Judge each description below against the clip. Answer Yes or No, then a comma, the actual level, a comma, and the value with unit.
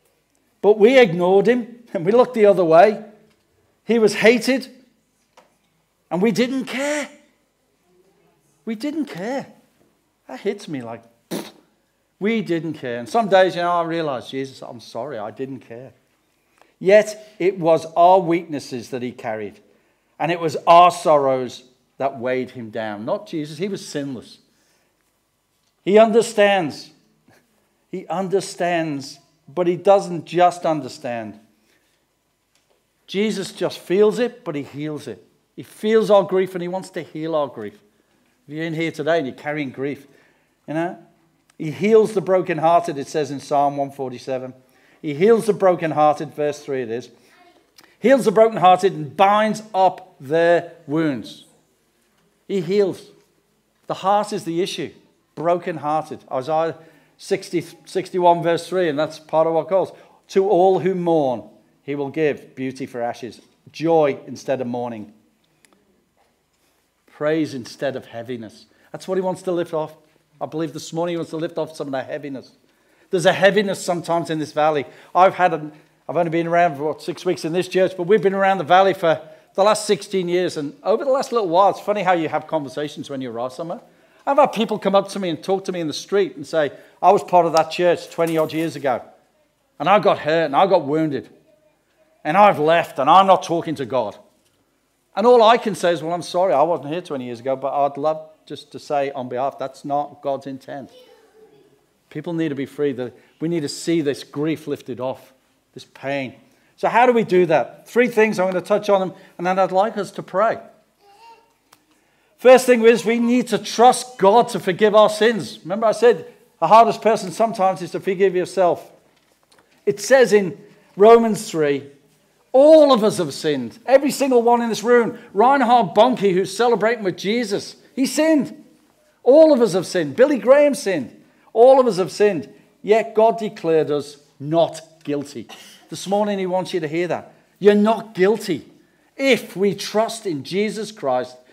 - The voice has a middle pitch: Yes, medium, 175 Hz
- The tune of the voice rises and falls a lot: Yes, wide, 5.7 semitones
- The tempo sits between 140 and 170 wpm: No, average, 180 wpm